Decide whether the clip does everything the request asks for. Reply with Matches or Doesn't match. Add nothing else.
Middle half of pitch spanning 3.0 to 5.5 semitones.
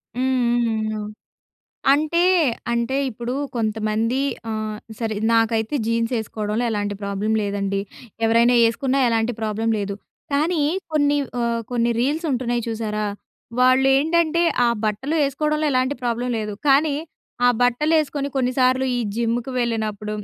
Matches